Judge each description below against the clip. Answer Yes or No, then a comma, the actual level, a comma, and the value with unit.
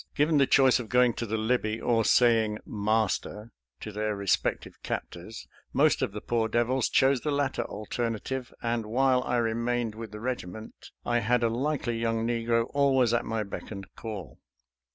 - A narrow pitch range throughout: Yes, narrow, 2.3 semitones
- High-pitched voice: No, low, 115 Hz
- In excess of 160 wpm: Yes, average, 175 wpm